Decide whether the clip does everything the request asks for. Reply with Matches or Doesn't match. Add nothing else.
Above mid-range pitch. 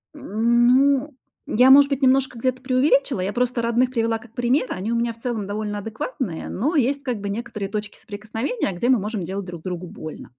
Matches